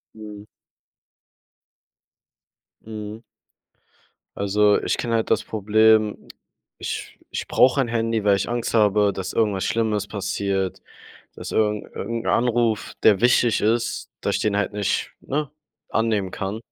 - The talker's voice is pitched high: No, low, 110 Hz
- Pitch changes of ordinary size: No, narrow, 1.9 semitones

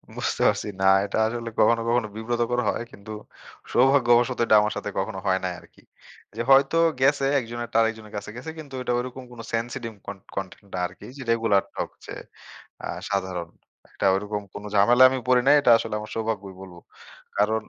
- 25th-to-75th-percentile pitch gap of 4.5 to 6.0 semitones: No, average, 3.2 semitones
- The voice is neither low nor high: No, low, 115 Hz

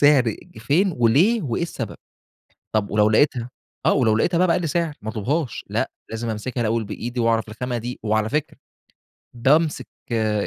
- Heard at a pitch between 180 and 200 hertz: No, low, 120 Hz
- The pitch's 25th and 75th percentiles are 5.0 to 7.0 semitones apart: Yes, average, 5.3 semitones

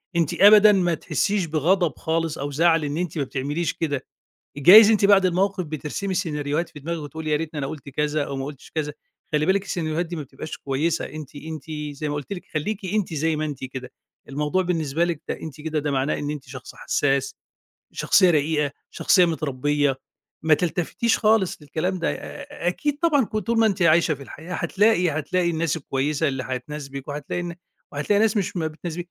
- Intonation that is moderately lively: Yes, average, 3.5 semitones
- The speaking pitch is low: No, medium, 160 Hz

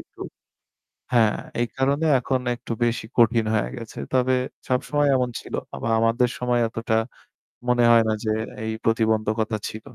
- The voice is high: No, low, 115 Hz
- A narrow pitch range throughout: Yes, narrow, 2.1 semitones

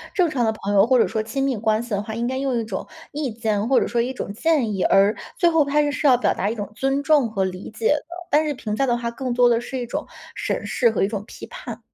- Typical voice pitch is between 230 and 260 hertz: Yes, high, 240 Hz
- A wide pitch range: No, average, 4.1 semitones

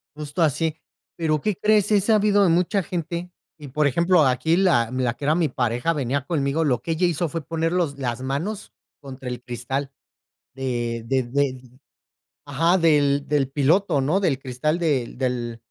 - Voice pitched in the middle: Yes, medium, 145 Hz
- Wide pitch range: No, average, 4.6 semitones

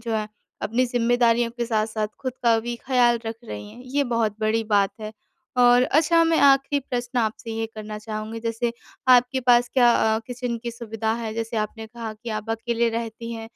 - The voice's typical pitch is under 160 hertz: No, high, 230 Hz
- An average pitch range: No, narrow, 1.7 semitones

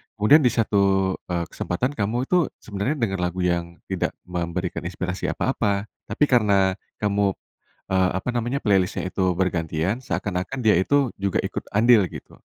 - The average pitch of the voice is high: No, low, 100 Hz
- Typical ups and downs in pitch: Yes, average, 3.7 semitones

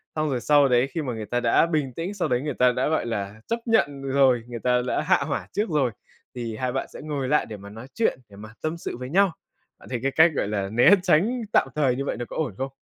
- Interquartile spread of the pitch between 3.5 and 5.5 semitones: Yes, average, 4.2 semitones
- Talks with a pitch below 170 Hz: Yes, low, 135 Hz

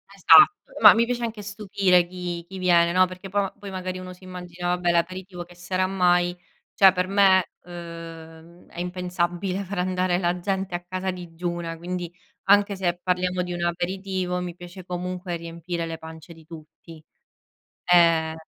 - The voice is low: No, medium, 180 Hz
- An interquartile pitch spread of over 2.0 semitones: No, narrow, 1.4 semitones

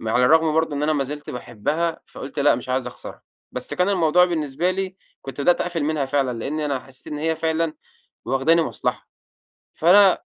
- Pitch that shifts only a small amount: No, average, 3.6 semitones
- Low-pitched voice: No, medium, 155 Hz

